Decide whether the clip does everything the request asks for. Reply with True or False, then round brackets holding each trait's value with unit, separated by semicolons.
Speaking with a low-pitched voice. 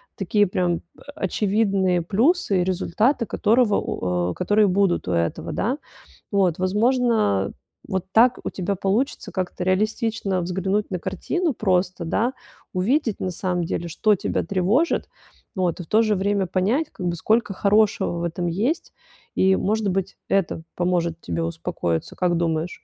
False (190 Hz)